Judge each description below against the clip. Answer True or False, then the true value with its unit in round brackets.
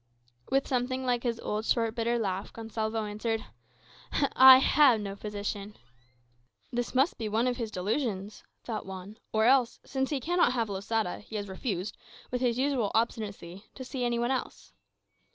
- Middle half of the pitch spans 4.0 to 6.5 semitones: False (3.2 semitones)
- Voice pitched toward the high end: True (230 Hz)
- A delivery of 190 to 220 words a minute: False (165 wpm)